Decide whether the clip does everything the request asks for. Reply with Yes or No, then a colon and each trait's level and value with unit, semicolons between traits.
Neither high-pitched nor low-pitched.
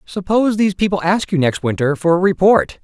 Yes: medium, 180 Hz